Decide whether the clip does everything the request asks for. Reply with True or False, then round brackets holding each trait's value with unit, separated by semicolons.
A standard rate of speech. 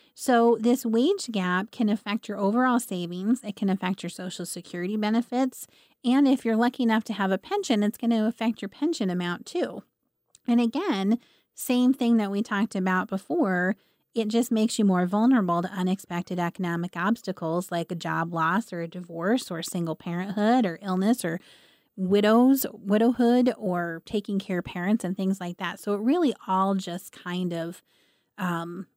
True (175 wpm)